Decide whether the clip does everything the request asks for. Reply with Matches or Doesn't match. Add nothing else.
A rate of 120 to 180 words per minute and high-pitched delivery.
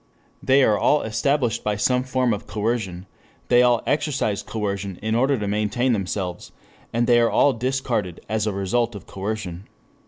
Doesn't match